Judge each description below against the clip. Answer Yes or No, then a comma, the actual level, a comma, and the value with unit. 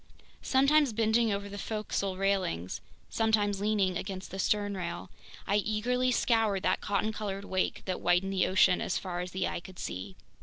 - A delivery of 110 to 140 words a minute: No, average, 165 wpm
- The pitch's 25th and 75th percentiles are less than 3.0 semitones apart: Yes, narrow, 2.6 semitones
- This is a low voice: No, high, 200 Hz